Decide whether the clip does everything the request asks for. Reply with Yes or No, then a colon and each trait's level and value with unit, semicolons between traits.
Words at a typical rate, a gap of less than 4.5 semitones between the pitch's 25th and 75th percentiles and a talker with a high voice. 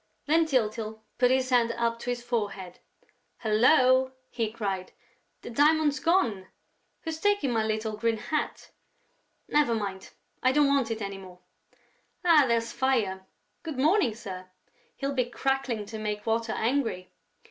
Yes: average, 145 wpm; average, 4.0 semitones; high, 235 Hz